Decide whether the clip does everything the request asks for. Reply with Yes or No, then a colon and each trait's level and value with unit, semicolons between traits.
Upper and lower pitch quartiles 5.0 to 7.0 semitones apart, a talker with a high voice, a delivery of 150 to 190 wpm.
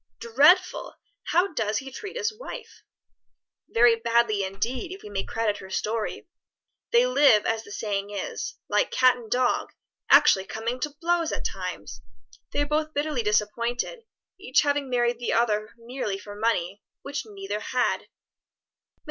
Yes: wide, 5.6 semitones; high, 235 Hz; average, 155 wpm